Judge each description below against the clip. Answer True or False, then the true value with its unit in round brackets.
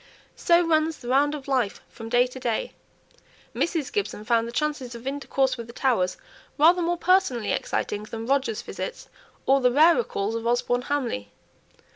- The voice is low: False (260 Hz)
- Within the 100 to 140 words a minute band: False (170 wpm)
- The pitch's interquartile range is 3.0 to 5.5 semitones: True (4.5 semitones)